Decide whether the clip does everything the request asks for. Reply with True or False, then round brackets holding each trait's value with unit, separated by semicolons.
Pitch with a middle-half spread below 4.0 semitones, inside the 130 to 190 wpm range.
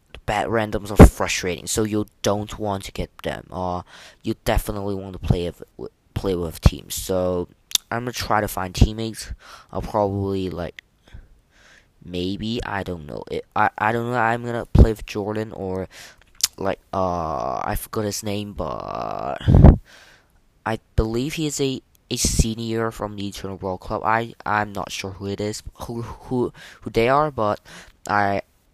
True (3.2 semitones; 165 wpm)